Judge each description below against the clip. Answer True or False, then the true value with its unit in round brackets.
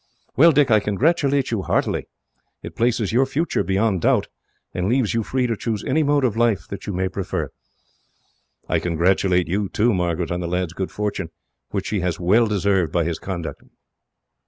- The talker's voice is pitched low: True (100 Hz)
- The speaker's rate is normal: True (180 wpm)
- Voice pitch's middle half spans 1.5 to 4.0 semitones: False (4.7 semitones)